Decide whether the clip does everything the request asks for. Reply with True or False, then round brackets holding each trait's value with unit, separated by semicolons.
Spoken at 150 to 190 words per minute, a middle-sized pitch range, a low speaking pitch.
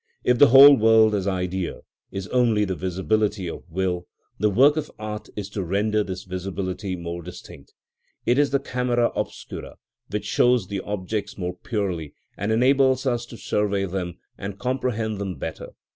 True (165 wpm; 4.2 semitones; 105 Hz)